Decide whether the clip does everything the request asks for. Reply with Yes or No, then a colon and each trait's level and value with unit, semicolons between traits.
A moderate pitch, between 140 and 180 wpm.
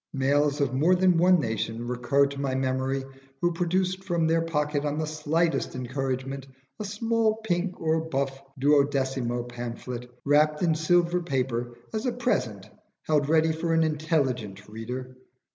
Yes: medium, 145 Hz; average, 150 wpm